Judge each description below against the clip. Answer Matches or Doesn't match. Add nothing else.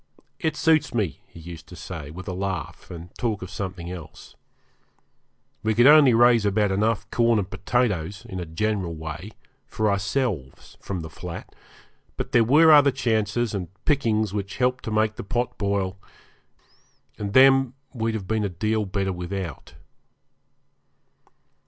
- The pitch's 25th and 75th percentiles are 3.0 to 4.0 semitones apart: Doesn't match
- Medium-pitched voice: Doesn't match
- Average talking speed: Matches